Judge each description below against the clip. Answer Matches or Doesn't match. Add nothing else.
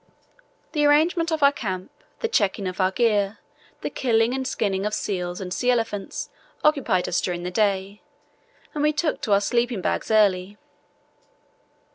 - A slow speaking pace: Doesn't match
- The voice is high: Matches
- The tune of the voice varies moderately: Doesn't match